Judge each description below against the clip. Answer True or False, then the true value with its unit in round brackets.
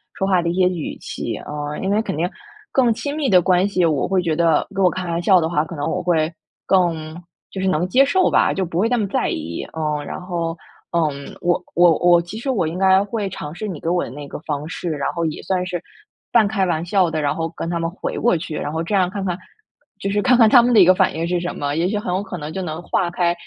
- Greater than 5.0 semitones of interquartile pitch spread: False (3.0 semitones)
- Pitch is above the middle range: False (175 Hz)